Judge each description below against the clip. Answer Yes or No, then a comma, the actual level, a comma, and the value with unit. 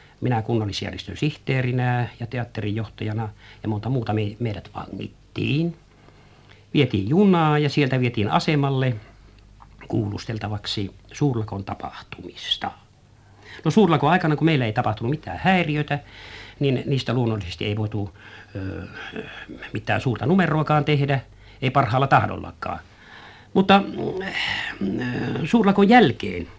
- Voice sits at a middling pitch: No, low, 115 Hz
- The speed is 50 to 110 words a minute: Yes, average, 100 wpm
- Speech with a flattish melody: No, wide, 5.6 semitones